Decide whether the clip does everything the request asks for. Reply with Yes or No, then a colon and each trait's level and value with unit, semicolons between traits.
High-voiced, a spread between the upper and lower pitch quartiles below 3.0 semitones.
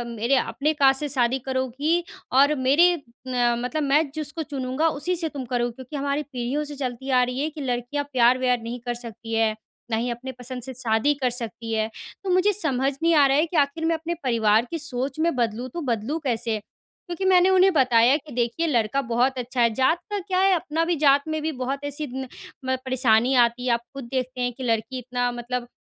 No: very high, 260 Hz; average, 3.7 semitones